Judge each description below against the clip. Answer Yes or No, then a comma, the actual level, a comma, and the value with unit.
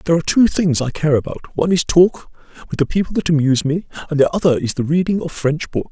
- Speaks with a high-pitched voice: No, medium, 160 Hz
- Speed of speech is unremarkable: No, fast, 245 wpm